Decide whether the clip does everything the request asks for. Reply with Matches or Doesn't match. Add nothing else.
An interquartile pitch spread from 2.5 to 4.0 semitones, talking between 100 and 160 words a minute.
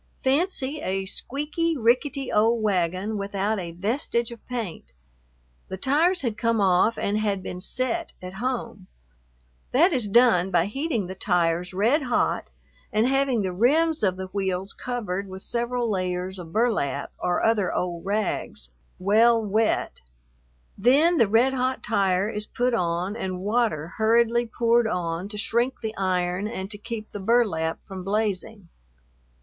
Doesn't match